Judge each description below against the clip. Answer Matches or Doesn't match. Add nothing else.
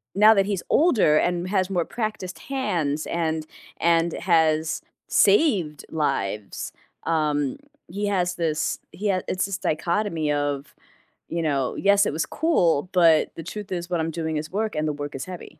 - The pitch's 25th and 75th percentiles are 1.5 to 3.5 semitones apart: Doesn't match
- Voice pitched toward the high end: Doesn't match